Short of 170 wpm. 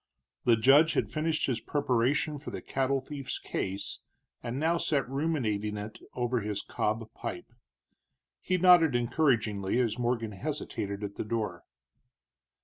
Yes: average, 140 wpm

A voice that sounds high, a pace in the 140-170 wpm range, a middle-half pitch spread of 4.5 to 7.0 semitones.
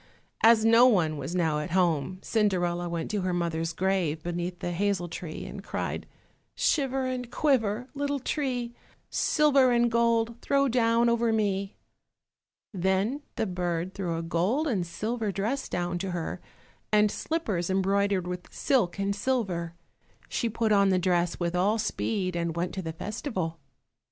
Yes: high, 195 Hz; average, 155 wpm; average, 5.0 semitones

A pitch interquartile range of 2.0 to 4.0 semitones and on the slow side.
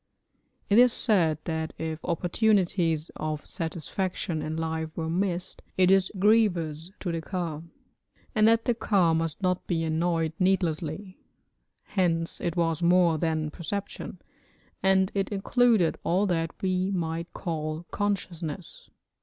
Yes: average, 3.0 semitones; slow, 130 wpm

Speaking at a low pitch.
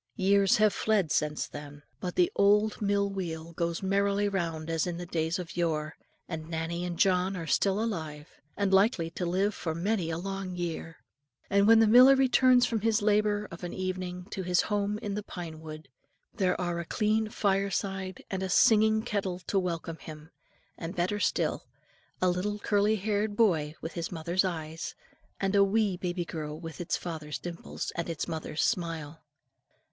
No: medium, 185 Hz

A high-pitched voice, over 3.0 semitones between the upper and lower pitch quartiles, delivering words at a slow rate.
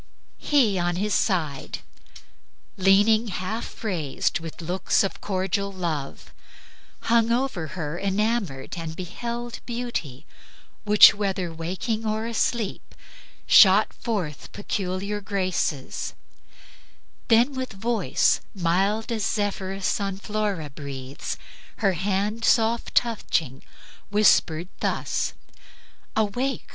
Yes: high, 195 Hz; average, 4.0 semitones; slow, 105 wpm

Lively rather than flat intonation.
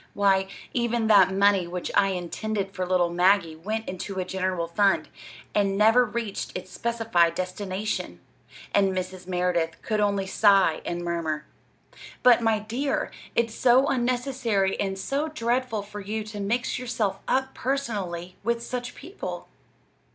No: average, 4.0 semitones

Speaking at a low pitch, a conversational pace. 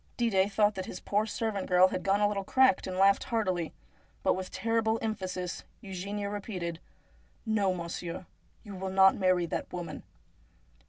No: high, 195 Hz; average, 165 wpm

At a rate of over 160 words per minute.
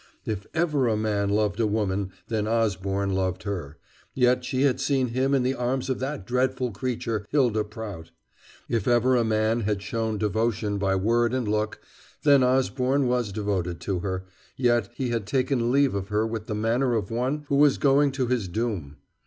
Yes: average, 185 wpm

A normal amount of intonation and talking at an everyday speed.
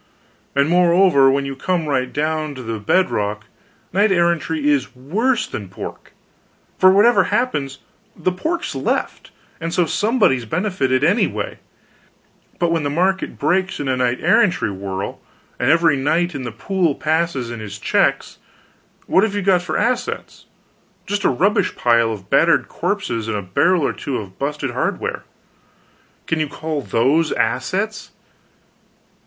No: wide, 6.4 semitones; average, 150 wpm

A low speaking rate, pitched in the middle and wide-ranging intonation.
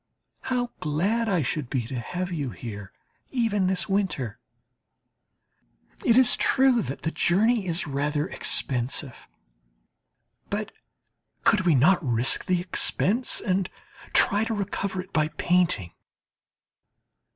Yes: slow, 120 wpm; medium, 180 Hz; wide, 6.3 semitones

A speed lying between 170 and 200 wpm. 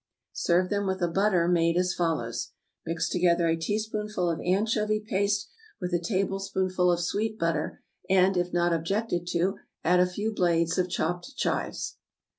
No: average, 160 wpm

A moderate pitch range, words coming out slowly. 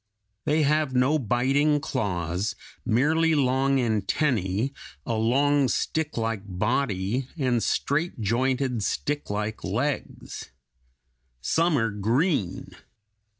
Yes: average, 5.0 semitones; slow, 90 wpm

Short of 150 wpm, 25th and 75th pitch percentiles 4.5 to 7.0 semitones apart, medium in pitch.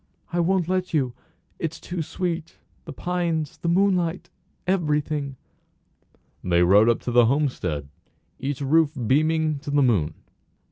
Yes: average, 140 wpm; average, 4.8 semitones; medium, 150 Hz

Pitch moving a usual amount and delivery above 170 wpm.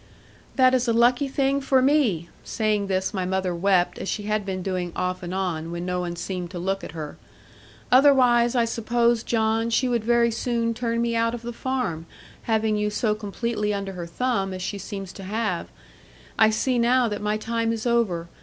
Yes: average, 4.0 semitones; average, 200 wpm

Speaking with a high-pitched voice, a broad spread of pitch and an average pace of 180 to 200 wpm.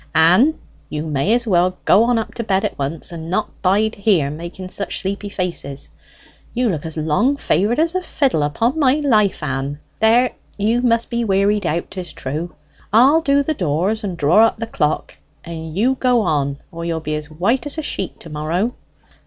Yes: high, 195 Hz; wide, 6.6 semitones; average, 195 wpm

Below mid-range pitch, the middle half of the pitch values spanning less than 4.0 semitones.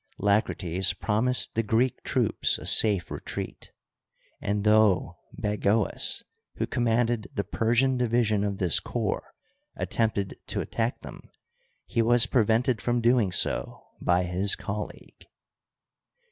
Yes: low, 110 Hz; average, 2.9 semitones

